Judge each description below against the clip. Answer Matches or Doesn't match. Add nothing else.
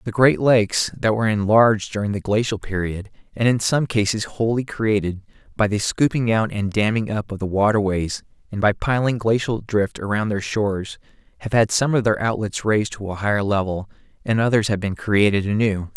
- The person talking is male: Matches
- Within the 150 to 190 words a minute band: Matches